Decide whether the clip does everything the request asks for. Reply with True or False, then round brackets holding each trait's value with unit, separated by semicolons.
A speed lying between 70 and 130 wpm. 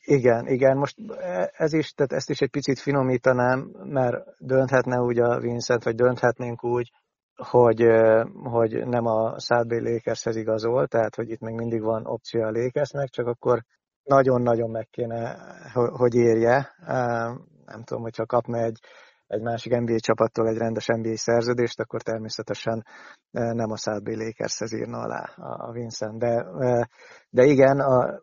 False (145 wpm)